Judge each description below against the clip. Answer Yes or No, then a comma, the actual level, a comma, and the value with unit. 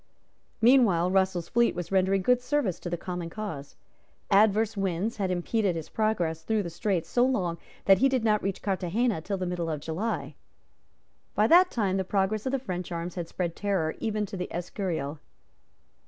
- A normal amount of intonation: Yes, average, 3.9 semitones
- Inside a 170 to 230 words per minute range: Yes, average, 185 wpm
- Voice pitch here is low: No, high, 190 Hz